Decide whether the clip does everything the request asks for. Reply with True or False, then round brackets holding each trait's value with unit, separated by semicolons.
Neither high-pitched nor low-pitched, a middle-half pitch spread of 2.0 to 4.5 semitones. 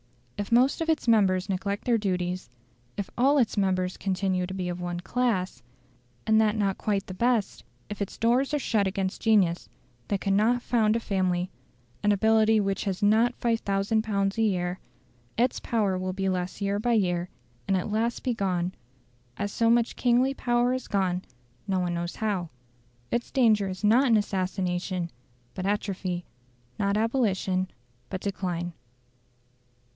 False (200 Hz; 3.4 semitones)